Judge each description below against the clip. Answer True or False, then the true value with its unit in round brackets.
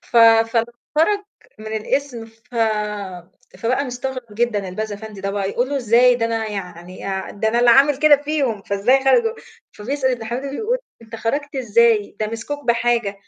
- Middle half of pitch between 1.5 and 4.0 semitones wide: True (3.6 semitones)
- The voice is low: False (235 Hz)